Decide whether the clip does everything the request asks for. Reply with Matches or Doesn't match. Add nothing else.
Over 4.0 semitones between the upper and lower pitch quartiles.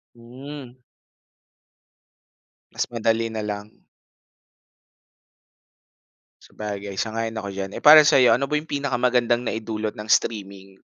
Doesn't match